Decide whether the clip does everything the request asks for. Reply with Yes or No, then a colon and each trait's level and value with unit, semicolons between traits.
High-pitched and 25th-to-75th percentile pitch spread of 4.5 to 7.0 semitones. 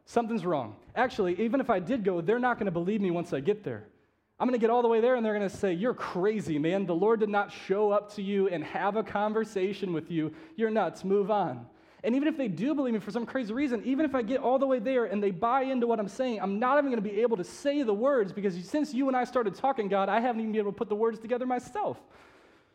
No: high, 220 Hz; average, 4.0 semitones